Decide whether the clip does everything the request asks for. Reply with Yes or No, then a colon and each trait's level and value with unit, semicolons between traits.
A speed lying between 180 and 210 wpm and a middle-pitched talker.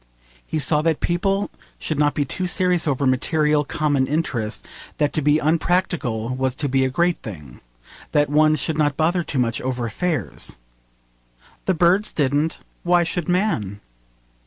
No: average, 160 wpm; medium, 150 Hz